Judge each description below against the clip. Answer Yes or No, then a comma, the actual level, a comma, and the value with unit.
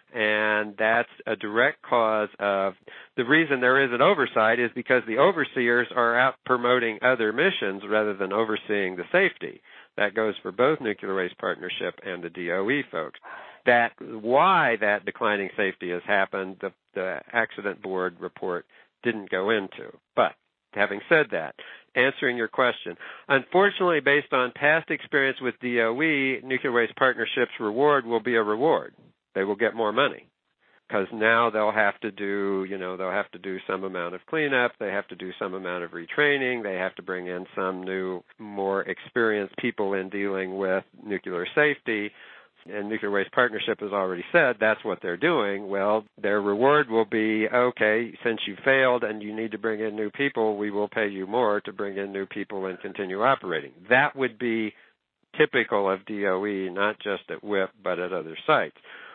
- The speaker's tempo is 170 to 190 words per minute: Yes, average, 175 wpm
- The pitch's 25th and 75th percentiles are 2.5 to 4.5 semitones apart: Yes, average, 4.0 semitones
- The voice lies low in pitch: Yes, low, 110 Hz